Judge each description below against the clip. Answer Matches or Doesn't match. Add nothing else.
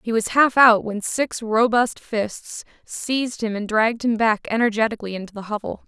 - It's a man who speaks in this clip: Doesn't match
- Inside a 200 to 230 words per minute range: Doesn't match